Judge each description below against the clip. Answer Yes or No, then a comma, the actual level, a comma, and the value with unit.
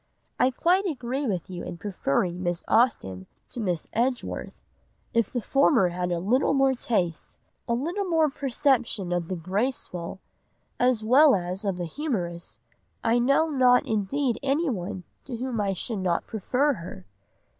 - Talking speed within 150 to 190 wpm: Yes, average, 155 wpm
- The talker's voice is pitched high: Yes, high, 230 Hz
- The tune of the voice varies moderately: No, wide, 6.8 semitones